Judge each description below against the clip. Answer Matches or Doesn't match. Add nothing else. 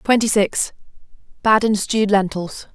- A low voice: Doesn't match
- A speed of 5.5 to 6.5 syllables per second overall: Doesn't match